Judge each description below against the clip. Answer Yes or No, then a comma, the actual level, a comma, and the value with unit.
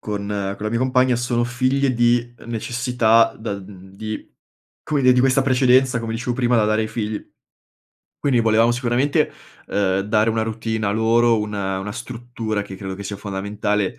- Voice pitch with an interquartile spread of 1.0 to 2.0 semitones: No, average, 2.8 semitones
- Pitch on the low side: Yes, low, 115 Hz